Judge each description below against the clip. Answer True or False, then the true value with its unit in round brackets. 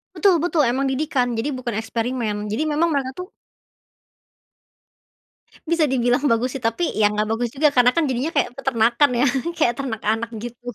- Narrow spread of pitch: False (3.6 semitones)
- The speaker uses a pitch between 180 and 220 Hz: False (250 Hz)